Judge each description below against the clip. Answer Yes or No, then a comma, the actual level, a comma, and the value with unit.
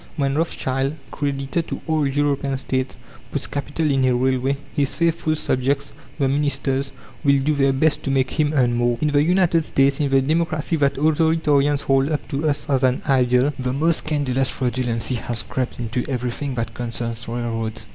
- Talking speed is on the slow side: No, average, 175 wpm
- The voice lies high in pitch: No, low, 135 Hz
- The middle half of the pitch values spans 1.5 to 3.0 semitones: Yes, narrow, 2.5 semitones